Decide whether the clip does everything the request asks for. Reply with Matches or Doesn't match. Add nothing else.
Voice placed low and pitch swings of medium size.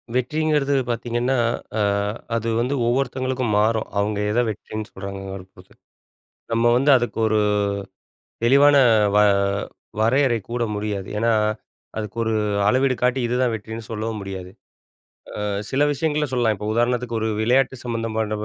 Matches